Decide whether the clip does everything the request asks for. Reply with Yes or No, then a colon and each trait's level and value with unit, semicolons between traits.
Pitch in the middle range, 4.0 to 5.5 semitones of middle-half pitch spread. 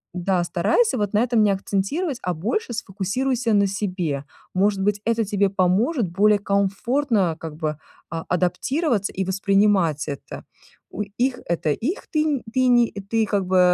No: high, 200 Hz; average, 4.3 semitones